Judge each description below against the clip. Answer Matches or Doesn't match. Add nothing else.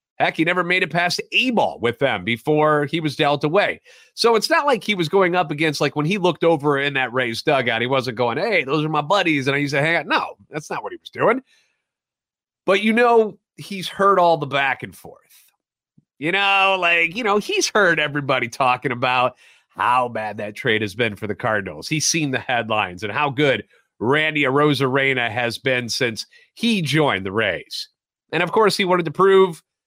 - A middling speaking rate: Doesn't match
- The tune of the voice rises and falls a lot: Matches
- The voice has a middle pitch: Matches